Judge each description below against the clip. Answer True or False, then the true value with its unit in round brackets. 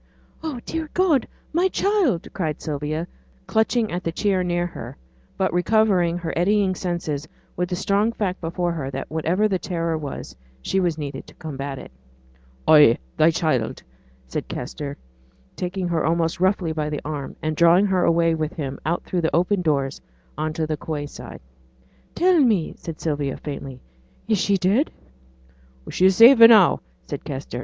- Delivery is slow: False (165 wpm)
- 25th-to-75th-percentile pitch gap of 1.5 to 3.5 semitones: False (4.2 semitones)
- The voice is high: False (170 Hz)